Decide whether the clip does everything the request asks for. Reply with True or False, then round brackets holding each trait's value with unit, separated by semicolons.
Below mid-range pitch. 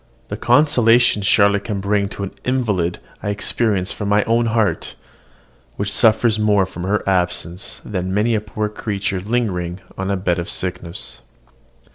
True (100 Hz)